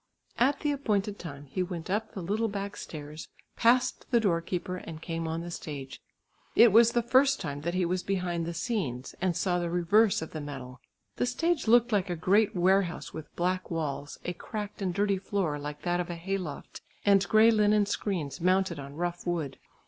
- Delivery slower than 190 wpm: No, average, 200 wpm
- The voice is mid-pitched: Yes, medium, 180 Hz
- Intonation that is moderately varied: Yes, average, 4.1 semitones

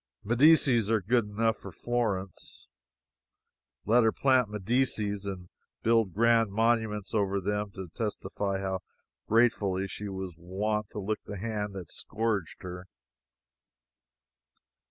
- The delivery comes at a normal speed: No, slow, 120 wpm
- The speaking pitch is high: No, low, 105 Hz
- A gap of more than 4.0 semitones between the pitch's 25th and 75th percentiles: No, average, 2.8 semitones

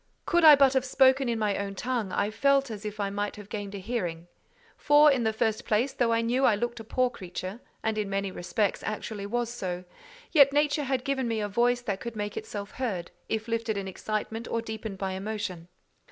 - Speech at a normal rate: No, fast, 220 wpm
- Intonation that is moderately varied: Yes, average, 3.4 semitones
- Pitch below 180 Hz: No, high, 220 Hz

